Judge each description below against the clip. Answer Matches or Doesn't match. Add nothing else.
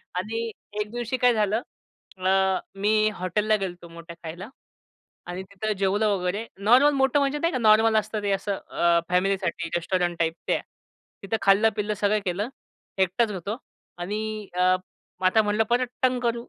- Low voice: Doesn't match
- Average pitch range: Matches